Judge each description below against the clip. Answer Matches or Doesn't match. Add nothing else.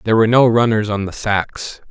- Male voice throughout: Matches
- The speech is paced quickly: Matches